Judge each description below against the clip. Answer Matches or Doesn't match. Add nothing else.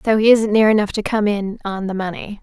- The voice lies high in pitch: Matches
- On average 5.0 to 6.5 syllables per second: Matches